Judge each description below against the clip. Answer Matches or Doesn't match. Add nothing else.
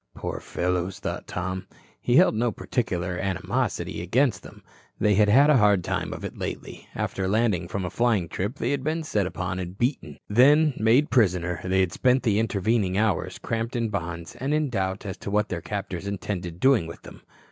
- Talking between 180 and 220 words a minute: Matches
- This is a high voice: Doesn't match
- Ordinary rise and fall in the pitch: Matches